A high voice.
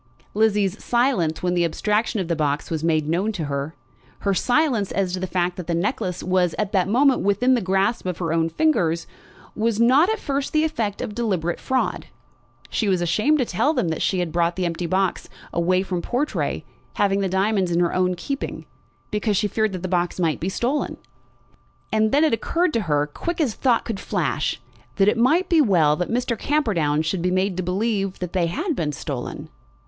Yes: high, 195 Hz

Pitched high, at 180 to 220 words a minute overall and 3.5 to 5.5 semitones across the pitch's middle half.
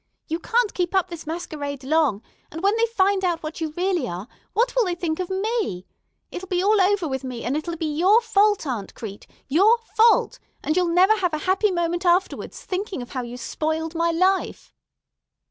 Yes: very high, 345 Hz; average, 200 wpm; average, 4.1 semitones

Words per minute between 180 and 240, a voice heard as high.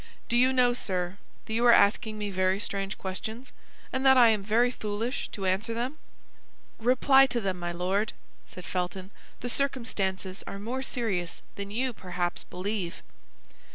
No: average, 160 wpm; high, 210 Hz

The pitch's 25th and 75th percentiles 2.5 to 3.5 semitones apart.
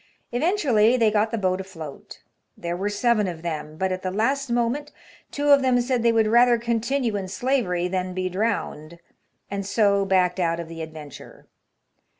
No: average, 4.8 semitones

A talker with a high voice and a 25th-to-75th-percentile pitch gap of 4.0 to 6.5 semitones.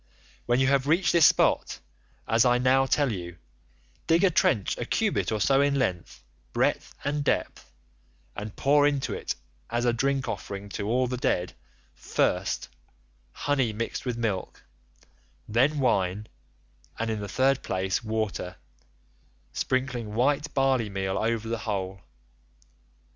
No: low, 120 Hz; average, 4.7 semitones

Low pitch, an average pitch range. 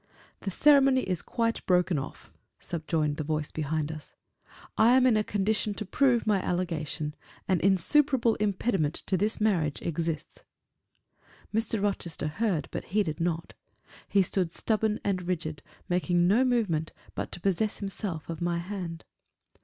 No: medium, 185 Hz; average, 4.7 semitones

